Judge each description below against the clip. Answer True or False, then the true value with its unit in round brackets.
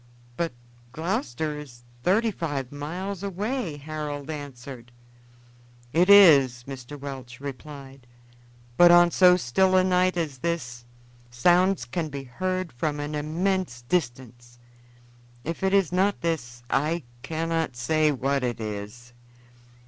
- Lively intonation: True (5.7 semitones)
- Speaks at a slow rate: True (125 wpm)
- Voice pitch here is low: False (150 Hz)